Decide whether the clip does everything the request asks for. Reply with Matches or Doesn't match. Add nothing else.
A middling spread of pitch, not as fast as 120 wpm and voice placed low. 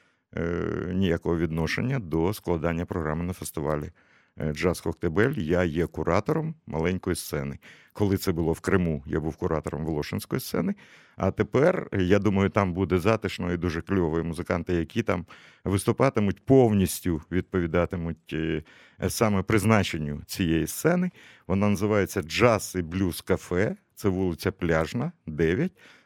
Doesn't match